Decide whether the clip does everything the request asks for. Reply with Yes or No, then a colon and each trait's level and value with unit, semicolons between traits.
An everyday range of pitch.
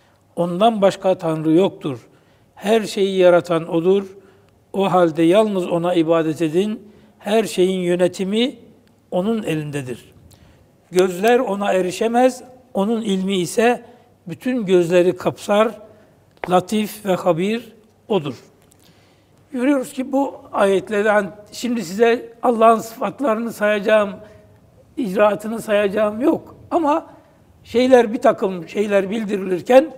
Yes: average, 4.2 semitones